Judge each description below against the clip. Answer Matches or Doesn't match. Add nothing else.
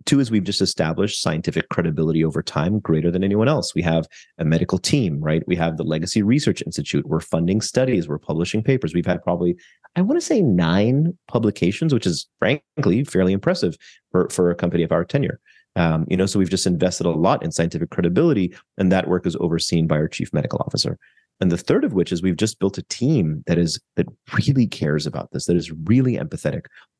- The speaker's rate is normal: Doesn't match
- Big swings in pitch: Doesn't match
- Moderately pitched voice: Doesn't match